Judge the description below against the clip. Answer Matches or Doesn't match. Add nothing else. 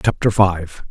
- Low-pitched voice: Matches